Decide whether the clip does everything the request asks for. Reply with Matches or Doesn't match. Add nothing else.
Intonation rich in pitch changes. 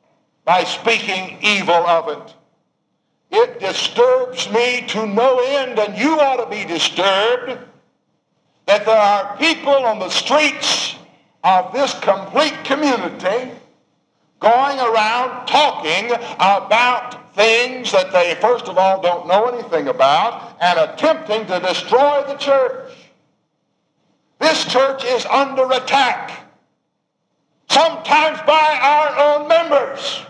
Matches